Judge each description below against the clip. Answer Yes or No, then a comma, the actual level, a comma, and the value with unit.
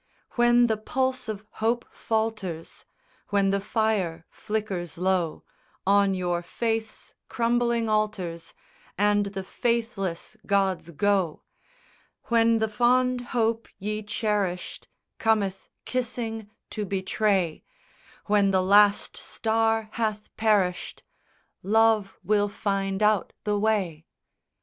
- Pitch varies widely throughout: No, narrow, 2.6 semitones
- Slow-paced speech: Yes, slow, 110 wpm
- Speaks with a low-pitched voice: No, high, 210 Hz